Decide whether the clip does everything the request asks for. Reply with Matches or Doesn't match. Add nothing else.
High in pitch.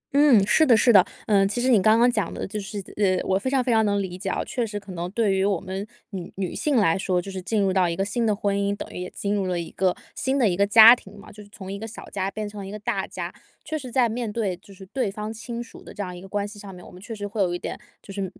Matches